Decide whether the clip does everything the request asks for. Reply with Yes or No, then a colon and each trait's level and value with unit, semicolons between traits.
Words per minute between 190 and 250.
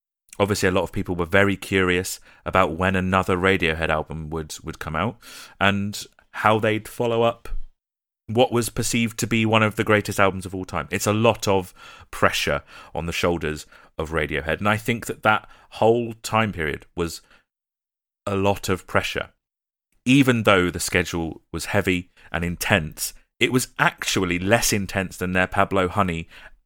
No: average, 170 wpm